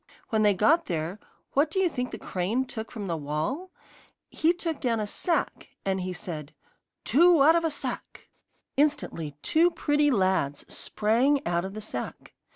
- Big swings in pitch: Yes, wide, 8.6 semitones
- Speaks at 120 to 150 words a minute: No, average, 170 wpm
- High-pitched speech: Yes, high, 225 Hz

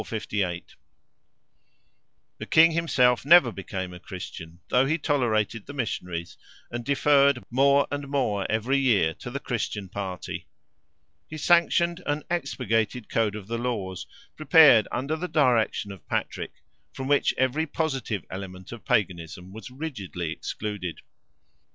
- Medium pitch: No, low, 120 Hz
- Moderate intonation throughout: No, wide, 6.3 semitones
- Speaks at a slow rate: Yes, slow, 130 wpm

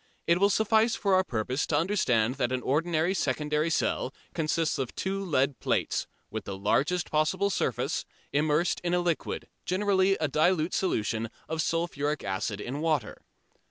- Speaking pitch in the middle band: Yes, medium, 155 Hz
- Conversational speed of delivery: Yes, average, 160 wpm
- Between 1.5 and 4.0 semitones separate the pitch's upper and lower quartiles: No, average, 5.3 semitones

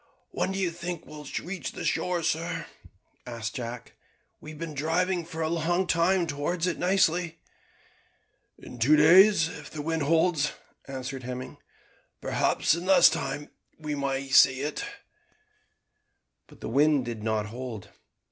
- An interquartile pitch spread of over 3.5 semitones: Yes, average, 4.1 semitones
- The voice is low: No, medium, 155 Hz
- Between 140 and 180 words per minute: Yes, average, 150 wpm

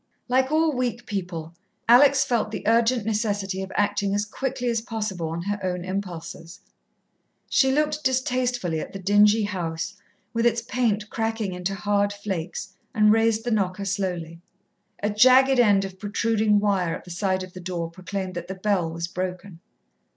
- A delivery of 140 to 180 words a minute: Yes, average, 165 wpm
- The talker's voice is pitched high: Yes, high, 205 Hz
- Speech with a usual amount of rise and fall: Yes, average, 3.8 semitones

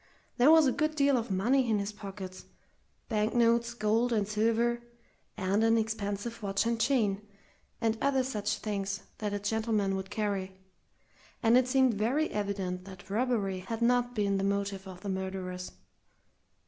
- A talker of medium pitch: No, high, 215 Hz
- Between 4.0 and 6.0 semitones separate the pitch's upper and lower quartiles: No, average, 3.2 semitones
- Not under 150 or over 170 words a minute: Yes, average, 160 wpm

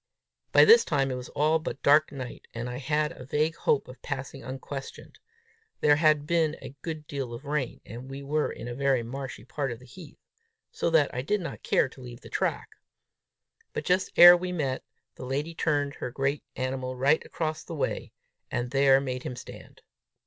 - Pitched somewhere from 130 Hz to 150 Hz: Yes, medium, 140 Hz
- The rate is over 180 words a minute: Yes, average, 200 wpm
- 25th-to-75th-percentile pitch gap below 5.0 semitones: Yes, average, 3.0 semitones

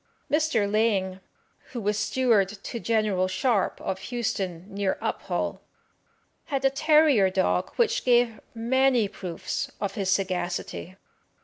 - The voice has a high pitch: Yes, high, 215 Hz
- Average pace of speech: No, slow, 120 wpm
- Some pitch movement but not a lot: Yes, average, 4.9 semitones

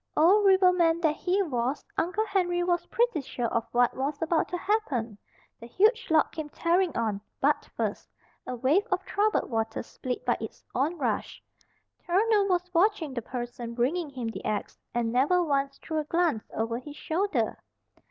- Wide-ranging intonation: Yes, wide, 6.7 semitones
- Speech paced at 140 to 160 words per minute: No, average, 170 wpm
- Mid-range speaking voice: No, very high, 315 Hz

